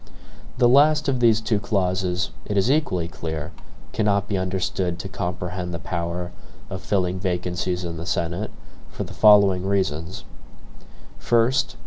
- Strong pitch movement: No, average, 3.0 semitones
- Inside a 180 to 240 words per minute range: No, average, 140 wpm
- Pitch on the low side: Yes, very low, 95 Hz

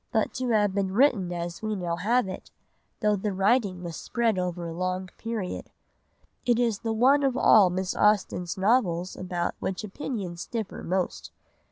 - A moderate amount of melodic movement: Yes, average, 3.9 semitones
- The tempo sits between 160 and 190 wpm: Yes, average, 170 wpm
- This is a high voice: Yes, high, 195 Hz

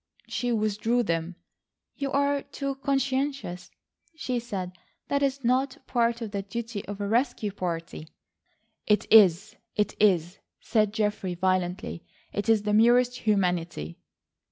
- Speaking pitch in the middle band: No, high, 215 Hz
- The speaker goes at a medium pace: No, slow, 130 wpm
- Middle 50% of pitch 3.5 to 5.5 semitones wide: Yes, average, 4.8 semitones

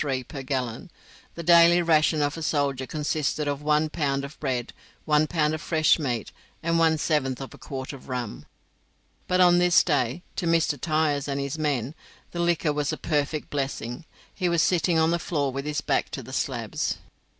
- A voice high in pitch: No, medium, 150 Hz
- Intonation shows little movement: No, average, 3.2 semitones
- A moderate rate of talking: Yes, average, 190 wpm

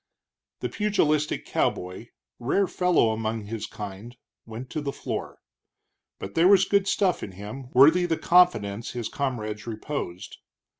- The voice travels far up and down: Yes, wide, 7.4 semitones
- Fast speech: No, average, 140 wpm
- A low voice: Yes, low, 125 Hz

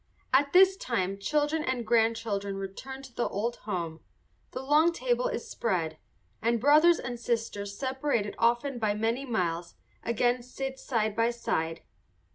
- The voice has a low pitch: No, high, 235 Hz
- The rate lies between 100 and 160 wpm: Yes, average, 145 wpm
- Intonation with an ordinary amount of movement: Yes, average, 4.7 semitones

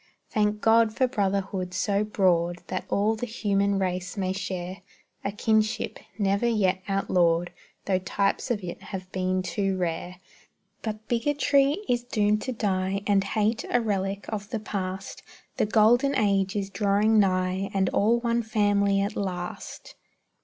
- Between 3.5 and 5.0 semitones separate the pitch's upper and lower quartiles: No, narrow, 2.5 semitones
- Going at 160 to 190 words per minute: No, average, 150 wpm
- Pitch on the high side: Yes, high, 200 Hz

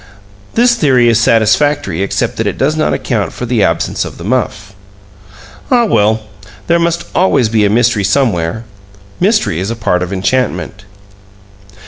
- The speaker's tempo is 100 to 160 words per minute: Yes, average, 155 wpm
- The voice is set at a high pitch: No, low, 115 Hz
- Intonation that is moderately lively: No, wide, 6.3 semitones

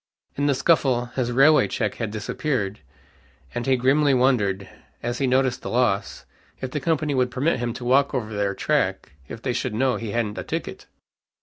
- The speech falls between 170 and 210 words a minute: Yes, average, 190 wpm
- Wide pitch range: No, average, 2.7 semitones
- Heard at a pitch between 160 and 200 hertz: No, low, 125 Hz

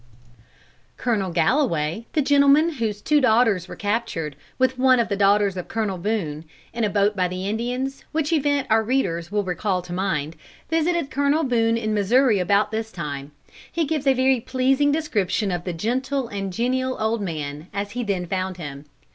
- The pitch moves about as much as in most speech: No, wide, 5.8 semitones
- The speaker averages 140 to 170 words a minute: No, average, 180 wpm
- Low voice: No, high, 220 Hz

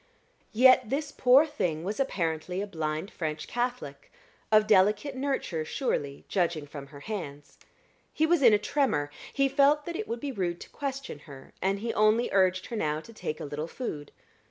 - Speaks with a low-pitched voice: No, high, 205 Hz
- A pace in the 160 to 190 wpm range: Yes, average, 180 wpm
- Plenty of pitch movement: Yes, wide, 8.9 semitones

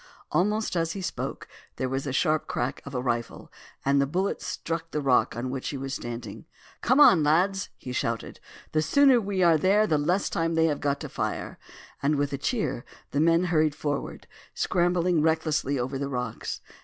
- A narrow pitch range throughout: No, average, 4.5 semitones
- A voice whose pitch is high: No, medium, 155 Hz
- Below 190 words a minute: No, average, 195 wpm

